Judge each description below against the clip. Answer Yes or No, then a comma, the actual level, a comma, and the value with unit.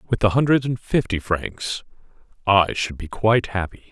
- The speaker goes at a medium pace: Yes, average, 170 wpm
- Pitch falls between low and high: No, low, 105 Hz